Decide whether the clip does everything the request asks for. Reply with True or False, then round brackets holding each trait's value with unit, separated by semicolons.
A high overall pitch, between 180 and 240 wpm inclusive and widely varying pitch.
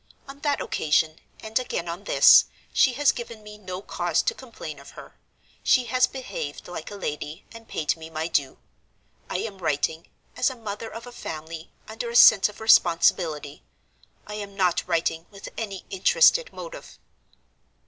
False (200 Hz; 165 wpm; 6.2 semitones)